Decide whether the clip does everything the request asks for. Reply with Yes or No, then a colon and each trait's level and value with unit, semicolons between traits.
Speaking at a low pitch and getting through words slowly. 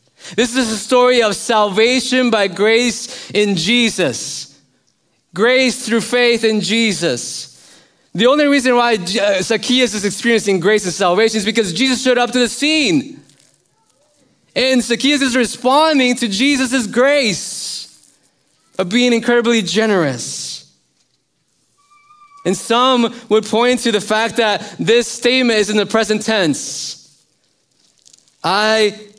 No: high, 225 Hz; slow, 125 wpm